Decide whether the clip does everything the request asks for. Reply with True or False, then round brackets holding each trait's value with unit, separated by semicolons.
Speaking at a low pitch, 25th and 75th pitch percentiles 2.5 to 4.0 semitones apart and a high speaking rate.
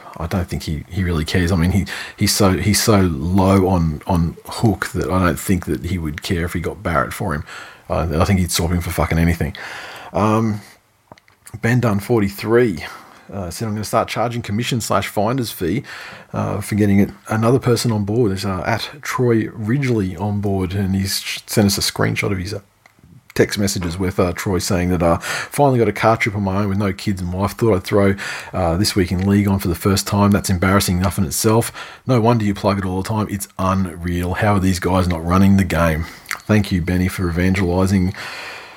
True (100 Hz; 2.9 semitones; 220 wpm)